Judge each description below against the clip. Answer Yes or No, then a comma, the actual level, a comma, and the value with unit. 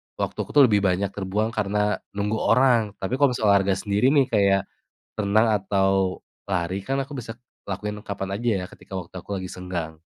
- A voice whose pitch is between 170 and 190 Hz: No, low, 100 Hz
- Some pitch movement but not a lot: No, narrow, 2.2 semitones